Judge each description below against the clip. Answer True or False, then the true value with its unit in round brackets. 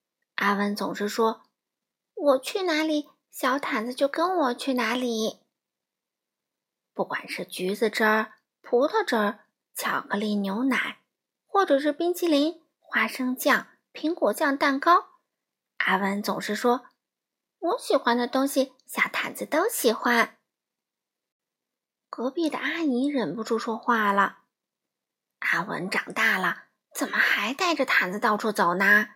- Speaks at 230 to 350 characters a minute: False (190 characters per minute)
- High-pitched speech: True (255 Hz)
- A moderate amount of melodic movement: False (6.1 semitones)